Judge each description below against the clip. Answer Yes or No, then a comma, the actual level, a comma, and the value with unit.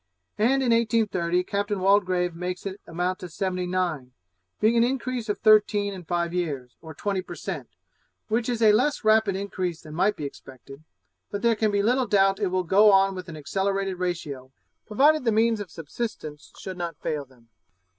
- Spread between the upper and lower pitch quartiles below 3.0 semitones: No, average, 3.9 semitones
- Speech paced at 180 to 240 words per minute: Yes, average, 185 wpm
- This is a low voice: No, high, 195 Hz